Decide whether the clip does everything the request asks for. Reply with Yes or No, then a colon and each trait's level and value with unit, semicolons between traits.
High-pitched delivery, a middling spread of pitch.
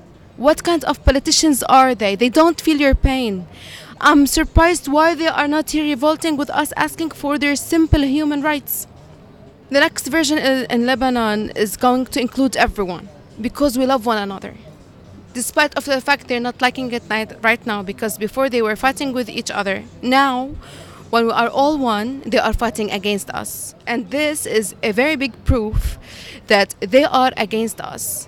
Yes: very high, 260 Hz; average, 4.5 semitones